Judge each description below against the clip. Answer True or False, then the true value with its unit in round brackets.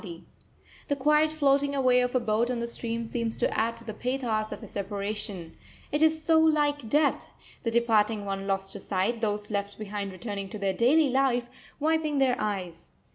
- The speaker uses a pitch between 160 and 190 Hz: False (235 Hz)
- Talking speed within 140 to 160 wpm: False (190 wpm)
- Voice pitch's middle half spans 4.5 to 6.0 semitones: True (5.0 semitones)